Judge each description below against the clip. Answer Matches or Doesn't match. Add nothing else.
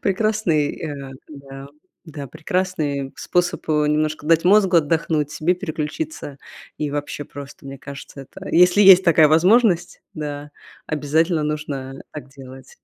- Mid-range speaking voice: Matches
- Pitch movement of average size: Matches